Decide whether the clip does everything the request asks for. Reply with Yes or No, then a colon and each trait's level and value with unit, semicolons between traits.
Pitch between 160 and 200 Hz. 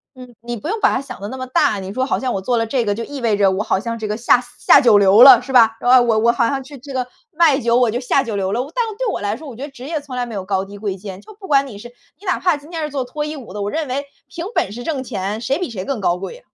No: high, 245 Hz